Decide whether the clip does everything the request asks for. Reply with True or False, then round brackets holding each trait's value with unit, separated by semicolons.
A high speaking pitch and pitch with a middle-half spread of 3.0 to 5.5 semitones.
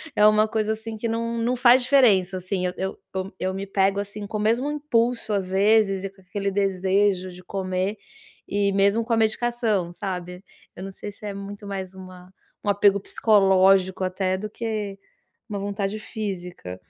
False (200 Hz; 2.4 semitones)